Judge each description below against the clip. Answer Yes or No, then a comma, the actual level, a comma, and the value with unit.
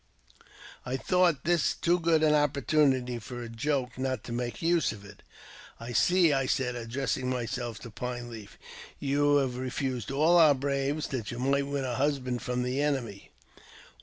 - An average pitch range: Yes, average, 3.0 semitones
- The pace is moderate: Yes, average, 170 wpm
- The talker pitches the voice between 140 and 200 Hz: No, low, 130 Hz